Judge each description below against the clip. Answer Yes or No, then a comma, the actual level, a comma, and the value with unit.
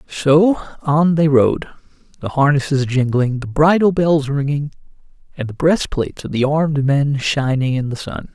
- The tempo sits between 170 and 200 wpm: No, average, 160 wpm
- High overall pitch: No, medium, 145 Hz